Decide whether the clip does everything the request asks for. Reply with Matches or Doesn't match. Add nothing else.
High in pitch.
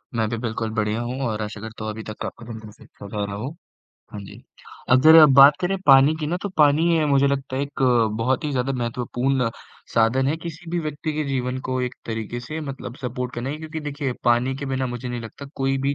Doesn't match